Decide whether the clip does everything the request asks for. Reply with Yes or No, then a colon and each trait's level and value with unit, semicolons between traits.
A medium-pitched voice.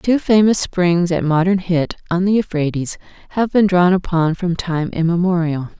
Yes: medium, 175 Hz